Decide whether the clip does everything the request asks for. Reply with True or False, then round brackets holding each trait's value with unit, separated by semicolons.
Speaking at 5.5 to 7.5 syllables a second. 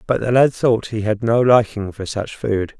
False (4.5 syllables/s)